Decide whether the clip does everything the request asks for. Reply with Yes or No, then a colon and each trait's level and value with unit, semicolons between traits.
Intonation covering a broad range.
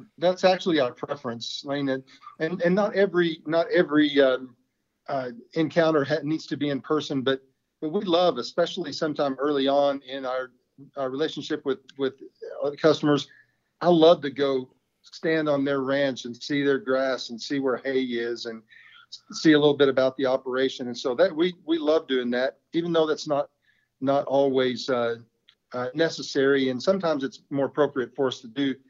No: average, 3.4 semitones